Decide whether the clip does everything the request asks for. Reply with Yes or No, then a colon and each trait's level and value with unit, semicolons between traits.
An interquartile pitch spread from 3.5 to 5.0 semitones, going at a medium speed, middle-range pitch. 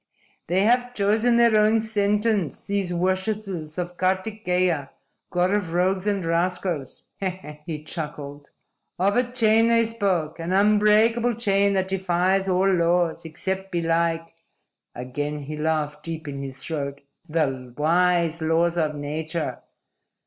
No: average, 4.1 semitones; slow, 125 wpm; medium, 180 Hz